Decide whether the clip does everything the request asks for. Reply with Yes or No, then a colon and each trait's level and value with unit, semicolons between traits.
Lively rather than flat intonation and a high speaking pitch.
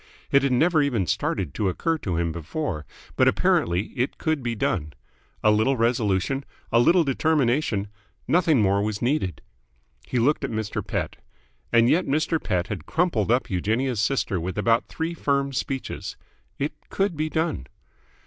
No: wide, 6.9 semitones; low, 120 Hz